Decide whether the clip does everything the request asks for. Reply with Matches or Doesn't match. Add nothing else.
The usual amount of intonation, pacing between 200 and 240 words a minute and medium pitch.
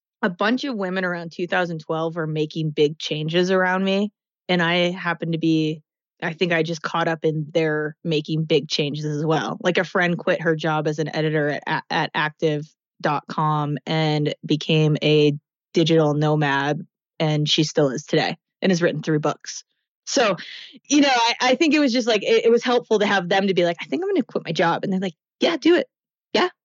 Matches